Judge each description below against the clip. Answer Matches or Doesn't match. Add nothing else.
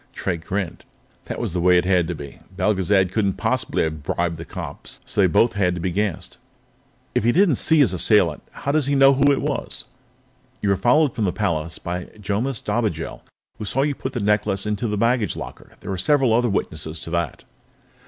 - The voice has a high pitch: Doesn't match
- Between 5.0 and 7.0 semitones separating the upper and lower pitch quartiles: Matches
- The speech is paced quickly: Matches